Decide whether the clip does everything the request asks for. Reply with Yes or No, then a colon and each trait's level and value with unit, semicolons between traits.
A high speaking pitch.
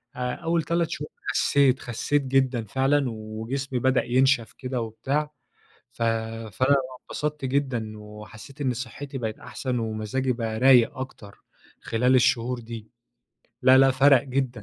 No: low, 130 Hz